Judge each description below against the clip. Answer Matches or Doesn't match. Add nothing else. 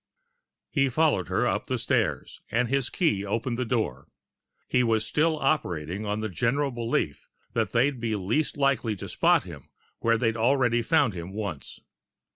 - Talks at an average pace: Matches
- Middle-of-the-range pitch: Doesn't match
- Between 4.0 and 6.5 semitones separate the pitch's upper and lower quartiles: Matches